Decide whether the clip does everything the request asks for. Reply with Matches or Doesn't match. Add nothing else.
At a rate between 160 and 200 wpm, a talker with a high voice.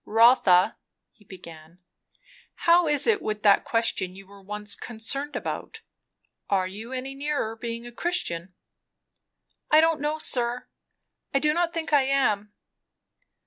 Doesn't match